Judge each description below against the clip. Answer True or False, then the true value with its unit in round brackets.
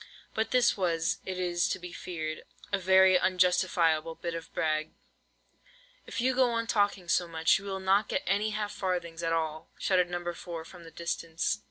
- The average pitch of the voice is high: False (180 Hz)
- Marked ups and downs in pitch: False (2.8 semitones)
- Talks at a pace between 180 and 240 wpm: True (185 wpm)